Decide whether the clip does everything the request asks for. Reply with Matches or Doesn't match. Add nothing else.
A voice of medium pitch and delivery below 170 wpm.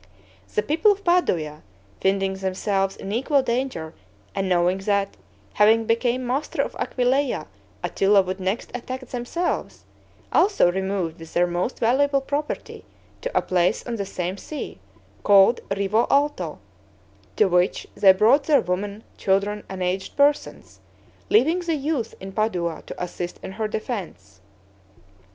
Doesn't match